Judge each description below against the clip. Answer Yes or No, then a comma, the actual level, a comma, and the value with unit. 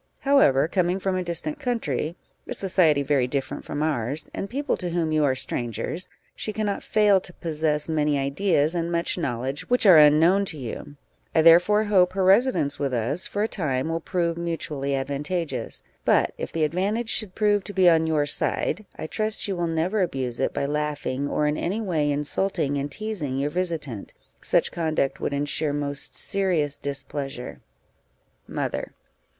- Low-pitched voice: No, medium, 160 Hz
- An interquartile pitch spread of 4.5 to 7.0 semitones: Yes, average, 4.8 semitones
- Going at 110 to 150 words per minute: No, average, 175 wpm